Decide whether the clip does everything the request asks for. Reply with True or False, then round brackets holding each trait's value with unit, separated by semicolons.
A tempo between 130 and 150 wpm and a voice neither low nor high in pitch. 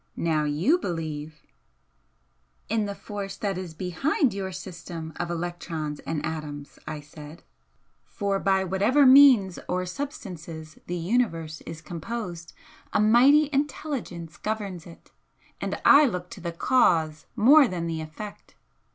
True (135 wpm; 180 Hz)